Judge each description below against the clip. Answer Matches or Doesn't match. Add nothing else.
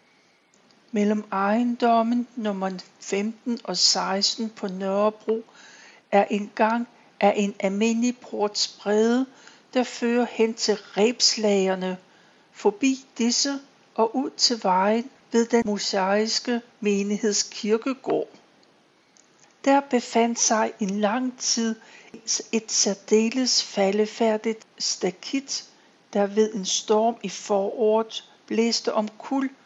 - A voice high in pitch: Matches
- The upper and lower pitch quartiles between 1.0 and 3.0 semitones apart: Matches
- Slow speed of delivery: Matches